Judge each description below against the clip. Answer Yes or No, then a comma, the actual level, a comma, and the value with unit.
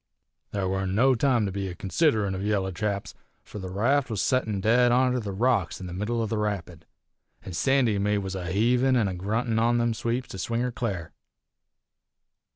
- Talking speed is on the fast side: Yes, fast, 210 wpm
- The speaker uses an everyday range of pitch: Yes, average, 3.9 semitones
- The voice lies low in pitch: Yes, low, 105 Hz